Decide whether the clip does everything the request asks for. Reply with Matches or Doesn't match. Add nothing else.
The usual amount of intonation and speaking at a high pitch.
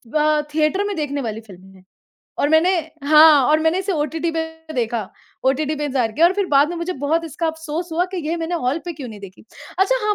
Matches